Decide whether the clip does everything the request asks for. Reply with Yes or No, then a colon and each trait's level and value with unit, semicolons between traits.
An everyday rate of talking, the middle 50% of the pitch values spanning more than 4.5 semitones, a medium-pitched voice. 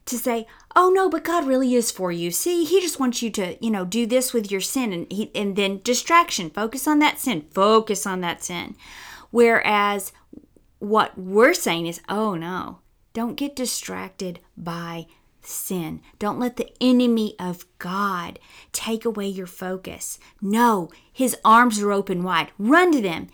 No: average, 170 wpm; average, 4.9 semitones; high, 215 Hz